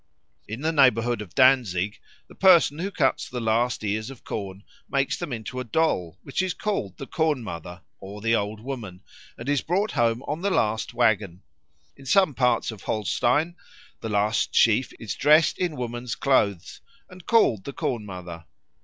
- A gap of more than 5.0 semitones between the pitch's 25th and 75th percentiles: Yes, wide, 5.5 semitones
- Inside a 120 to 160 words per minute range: No, average, 175 wpm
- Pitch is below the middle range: Yes, low, 120 Hz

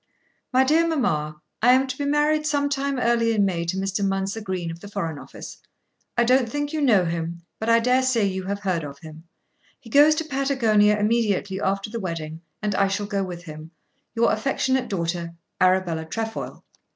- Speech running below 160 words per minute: No, average, 190 wpm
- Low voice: No, high, 205 Hz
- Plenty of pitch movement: Yes, wide, 6.2 semitones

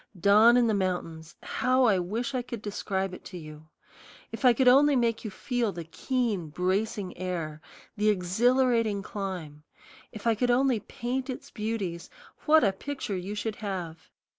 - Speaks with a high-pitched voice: Yes, high, 210 Hz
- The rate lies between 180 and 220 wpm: No, average, 165 wpm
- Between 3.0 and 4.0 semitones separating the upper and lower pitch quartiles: No, average, 5.0 semitones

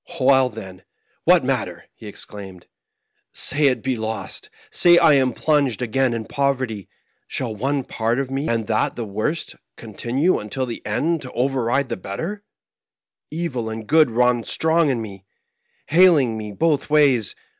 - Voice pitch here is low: Yes, low, 130 Hz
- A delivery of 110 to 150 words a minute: No, average, 160 wpm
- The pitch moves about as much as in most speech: Yes, average, 4.7 semitones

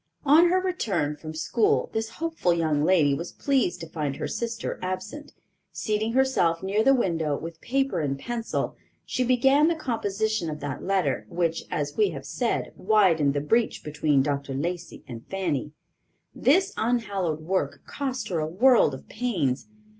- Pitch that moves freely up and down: Yes, wide, 7.8 semitones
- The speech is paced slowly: No, average, 160 wpm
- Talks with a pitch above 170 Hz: Yes, medium, 185 Hz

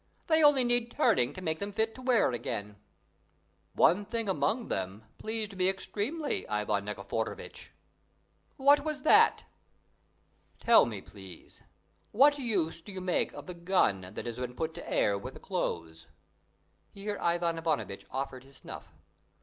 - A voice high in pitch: No, medium, 180 Hz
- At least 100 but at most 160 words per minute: Yes, average, 150 wpm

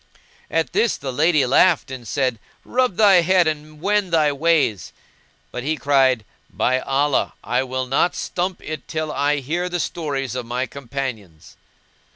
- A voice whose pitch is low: No, medium, 145 Hz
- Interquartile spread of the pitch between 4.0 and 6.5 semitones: Yes, average, 4.4 semitones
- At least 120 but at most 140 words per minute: No, average, 160 wpm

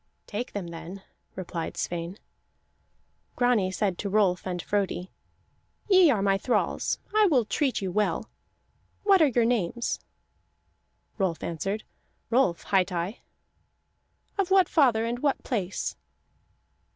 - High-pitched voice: Yes, high, 205 Hz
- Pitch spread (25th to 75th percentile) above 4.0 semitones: Yes, average, 5.2 semitones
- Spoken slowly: Yes, slow, 125 wpm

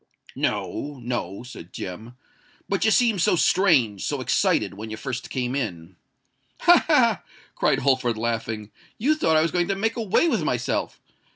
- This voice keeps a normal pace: Yes, average, 150 wpm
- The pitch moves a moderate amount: No, wide, 8.6 semitones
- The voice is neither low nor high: No, low, 125 Hz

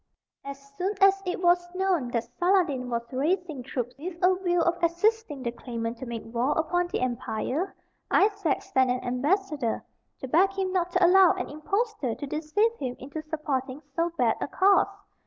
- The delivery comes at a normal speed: Yes, average, 175 wpm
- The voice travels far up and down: Yes, wide, 6.3 semitones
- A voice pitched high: Yes, very high, 315 Hz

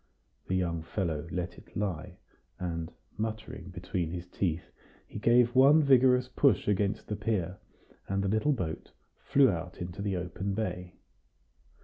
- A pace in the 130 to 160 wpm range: Yes, average, 145 wpm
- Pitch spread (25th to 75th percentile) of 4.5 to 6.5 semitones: No, average, 3.9 semitones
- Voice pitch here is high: No, very low, 95 Hz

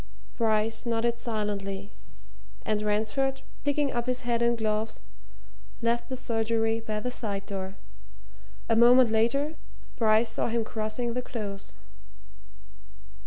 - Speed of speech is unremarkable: No, slow, 120 wpm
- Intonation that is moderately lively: No, narrow, 1.9 semitones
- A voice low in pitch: No, high, 225 Hz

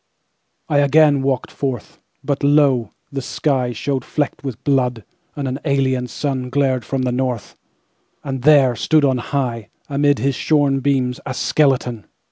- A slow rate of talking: Yes, slow, 125 wpm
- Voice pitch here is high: No, low, 135 Hz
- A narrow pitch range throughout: Yes, narrow, 2.2 semitones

